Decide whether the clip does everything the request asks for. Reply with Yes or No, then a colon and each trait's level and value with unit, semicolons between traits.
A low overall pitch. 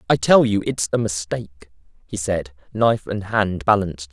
Yes: very low, 95 Hz